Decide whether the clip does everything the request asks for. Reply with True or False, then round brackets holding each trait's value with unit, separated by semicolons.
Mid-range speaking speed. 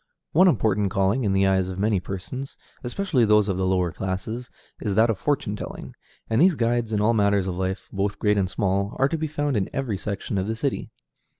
False (220 wpm)